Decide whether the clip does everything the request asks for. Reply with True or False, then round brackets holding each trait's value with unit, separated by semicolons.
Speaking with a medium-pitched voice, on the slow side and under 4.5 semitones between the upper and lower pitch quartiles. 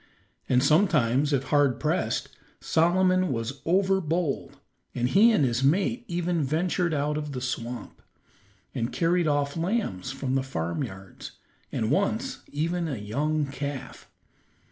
False (145 Hz; 130 wpm; 5.2 semitones)